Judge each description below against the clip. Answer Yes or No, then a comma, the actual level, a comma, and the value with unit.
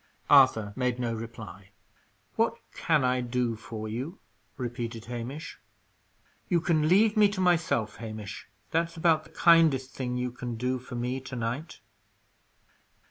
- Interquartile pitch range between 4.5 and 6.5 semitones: Yes, average, 5.3 semitones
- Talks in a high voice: No, low, 125 Hz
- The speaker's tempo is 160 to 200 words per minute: No, average, 140 wpm